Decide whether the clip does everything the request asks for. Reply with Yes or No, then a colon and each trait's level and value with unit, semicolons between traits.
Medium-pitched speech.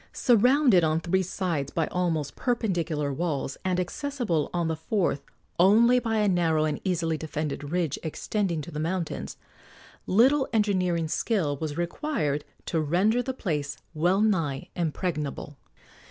Yes: medium, 175 Hz